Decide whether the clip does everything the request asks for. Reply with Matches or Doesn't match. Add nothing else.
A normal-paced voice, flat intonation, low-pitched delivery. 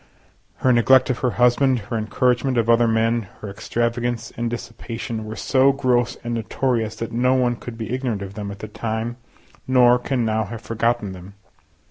Matches